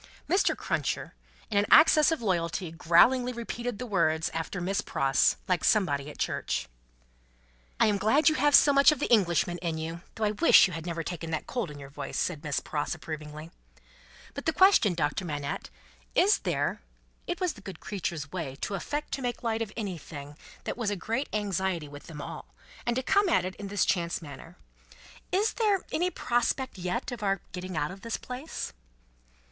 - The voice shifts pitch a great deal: Yes, wide, 7.0 semitones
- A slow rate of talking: No, average, 195 wpm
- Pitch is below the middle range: No, high, 195 Hz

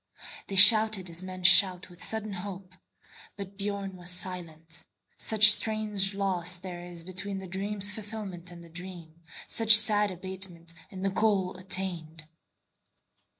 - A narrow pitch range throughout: Yes, narrow, 2.3 semitones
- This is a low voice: No, high, 190 Hz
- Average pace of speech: No, slow, 125 wpm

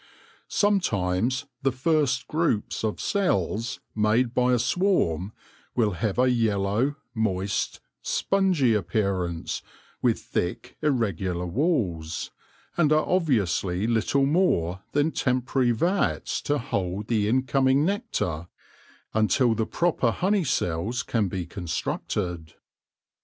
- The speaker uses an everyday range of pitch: No, wide, 6.7 semitones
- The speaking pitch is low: Yes, low, 115 Hz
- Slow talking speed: Yes, slow, 110 wpm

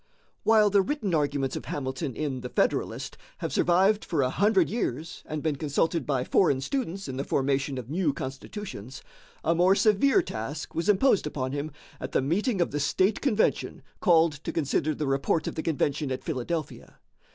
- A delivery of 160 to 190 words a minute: Yes, average, 180 wpm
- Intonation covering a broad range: Yes, wide, 5.8 semitones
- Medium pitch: Yes, medium, 155 Hz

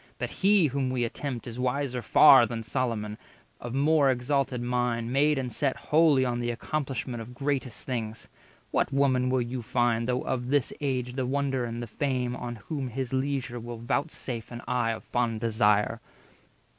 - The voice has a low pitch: Yes, low, 125 Hz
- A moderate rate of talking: Yes, average, 180 wpm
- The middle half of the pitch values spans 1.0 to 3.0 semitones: Yes, narrow, 2.4 semitones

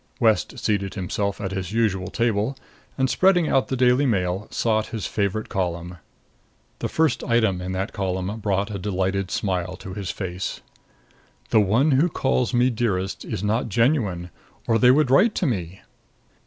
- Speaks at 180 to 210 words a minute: No, average, 165 wpm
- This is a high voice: No, low, 105 Hz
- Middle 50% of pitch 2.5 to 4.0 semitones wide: No, average, 4.5 semitones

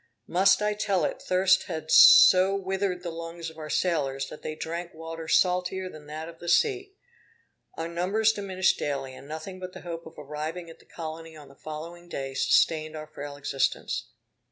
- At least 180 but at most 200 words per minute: Yes, average, 185 wpm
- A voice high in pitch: No, medium, 165 Hz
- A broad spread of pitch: No, average, 3.0 semitones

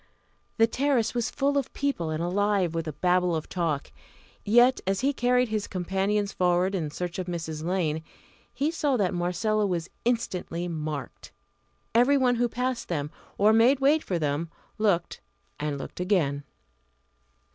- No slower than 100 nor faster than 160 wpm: Yes, average, 155 wpm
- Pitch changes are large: Yes, wide, 6.1 semitones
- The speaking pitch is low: No, high, 190 Hz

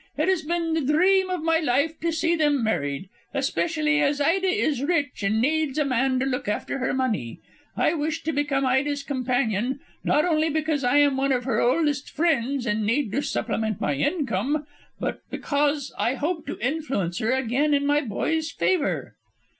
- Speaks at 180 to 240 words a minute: Yes, average, 185 wpm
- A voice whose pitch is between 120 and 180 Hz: No, very high, 285 Hz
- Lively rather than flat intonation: No, average, 3.8 semitones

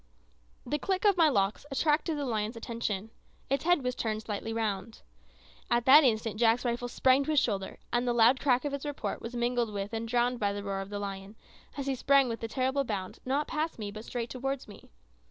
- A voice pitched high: Yes, high, 240 Hz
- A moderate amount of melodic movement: Yes, average, 4.1 semitones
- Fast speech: Yes, fast, 215 wpm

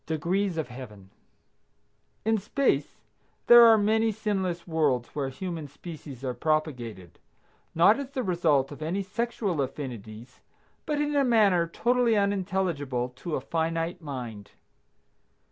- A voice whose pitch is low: No, medium, 165 Hz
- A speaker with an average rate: No, slow, 130 wpm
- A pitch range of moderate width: No, wide, 7.2 semitones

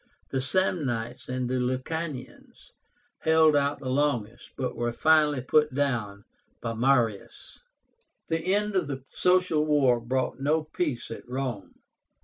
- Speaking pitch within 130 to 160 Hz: Yes, low, 135 Hz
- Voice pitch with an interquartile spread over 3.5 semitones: Yes, average, 4.0 semitones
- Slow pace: Yes, slow, 125 wpm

